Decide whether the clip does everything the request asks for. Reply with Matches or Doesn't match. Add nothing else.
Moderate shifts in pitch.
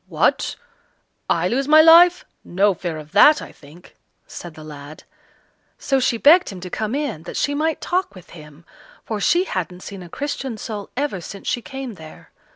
Doesn't match